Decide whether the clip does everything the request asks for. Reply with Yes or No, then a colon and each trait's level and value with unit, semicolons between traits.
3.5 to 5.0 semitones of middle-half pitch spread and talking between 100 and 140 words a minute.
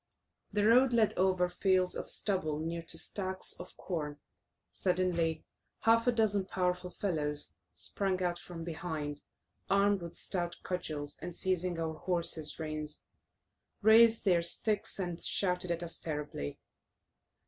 No: average, 3.0 semitones; slow, 135 wpm